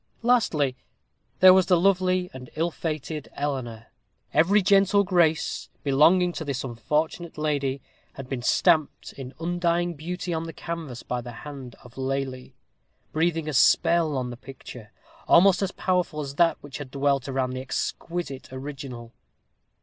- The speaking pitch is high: No, medium, 150 Hz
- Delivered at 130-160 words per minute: Yes, average, 150 wpm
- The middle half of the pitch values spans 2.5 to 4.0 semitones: No, average, 4.7 semitones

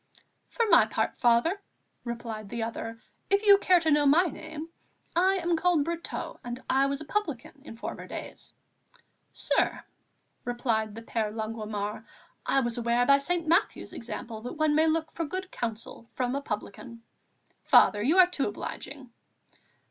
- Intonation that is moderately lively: No, wide, 6.1 semitones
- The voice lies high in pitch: Yes, very high, 270 Hz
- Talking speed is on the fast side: No, average, 160 wpm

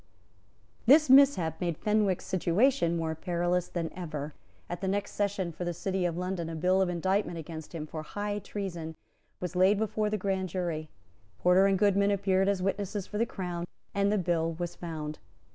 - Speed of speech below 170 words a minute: No, average, 180 wpm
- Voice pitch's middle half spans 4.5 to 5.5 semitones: No, average, 3.0 semitones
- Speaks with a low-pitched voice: No, medium, 185 Hz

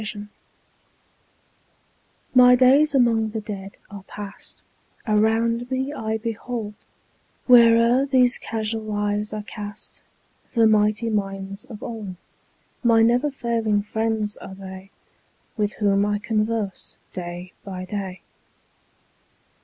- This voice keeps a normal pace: No, slow, 115 wpm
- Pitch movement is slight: Yes, narrow, 2.2 semitones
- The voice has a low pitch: No, high, 215 Hz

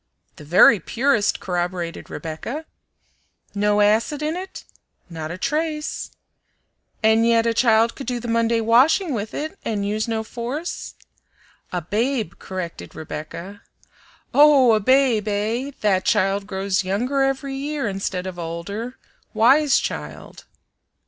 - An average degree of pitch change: No, wide, 5.7 semitones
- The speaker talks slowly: Yes, slow, 130 wpm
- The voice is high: Yes, high, 225 Hz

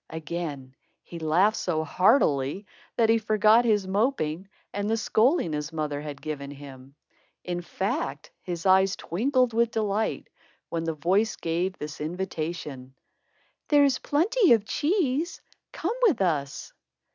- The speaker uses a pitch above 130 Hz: Yes, medium, 185 Hz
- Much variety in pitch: Yes, wide, 6.6 semitones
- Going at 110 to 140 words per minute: Yes, slow, 135 wpm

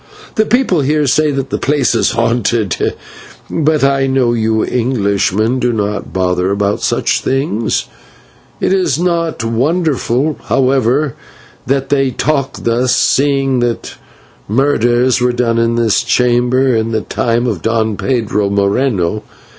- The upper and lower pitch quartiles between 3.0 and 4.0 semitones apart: Yes, average, 3.5 semitones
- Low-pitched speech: Yes, low, 125 Hz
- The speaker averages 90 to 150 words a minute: Yes, slow, 135 wpm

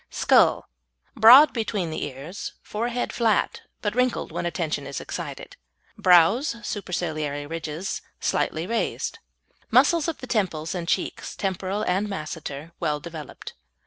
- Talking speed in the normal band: No, slow, 125 wpm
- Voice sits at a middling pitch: Yes, medium, 180 Hz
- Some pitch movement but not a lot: No, wide, 5.7 semitones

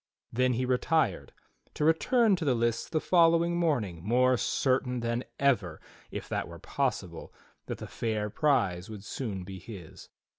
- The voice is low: Yes, low, 125 Hz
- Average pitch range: No, wide, 6.4 semitones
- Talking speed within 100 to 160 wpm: Yes, average, 155 wpm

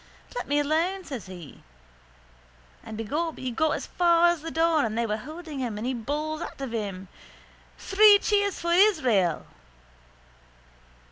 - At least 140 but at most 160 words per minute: Yes, average, 150 wpm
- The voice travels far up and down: Yes, wide, 6.9 semitones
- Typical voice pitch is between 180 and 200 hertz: No, very high, 300 Hz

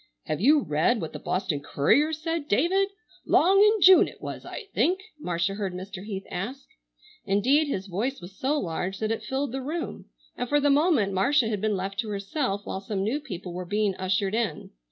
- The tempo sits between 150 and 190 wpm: No, average, 200 wpm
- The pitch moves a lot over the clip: Yes, wide, 7.1 semitones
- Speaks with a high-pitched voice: Yes, high, 215 Hz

